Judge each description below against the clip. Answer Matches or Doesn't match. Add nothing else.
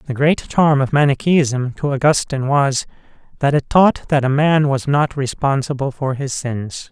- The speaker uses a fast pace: Doesn't match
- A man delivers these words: Matches